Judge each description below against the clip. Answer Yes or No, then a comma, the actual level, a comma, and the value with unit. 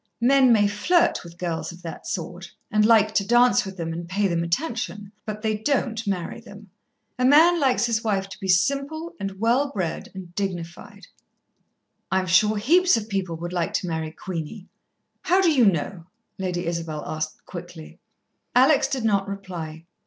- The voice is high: Yes, high, 200 Hz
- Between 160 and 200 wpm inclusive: Yes, average, 175 wpm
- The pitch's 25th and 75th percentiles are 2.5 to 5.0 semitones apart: No, wide, 5.4 semitones